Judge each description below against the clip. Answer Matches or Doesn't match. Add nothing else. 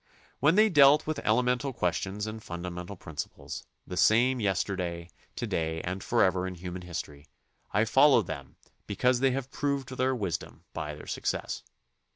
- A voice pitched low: Matches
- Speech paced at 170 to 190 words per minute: Doesn't match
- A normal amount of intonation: Doesn't match